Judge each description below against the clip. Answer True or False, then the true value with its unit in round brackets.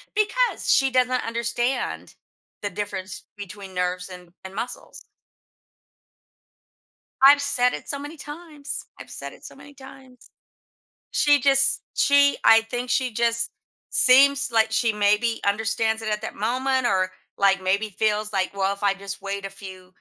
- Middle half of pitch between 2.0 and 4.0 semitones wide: False (5.0 semitones)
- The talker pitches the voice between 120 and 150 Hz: False (225 Hz)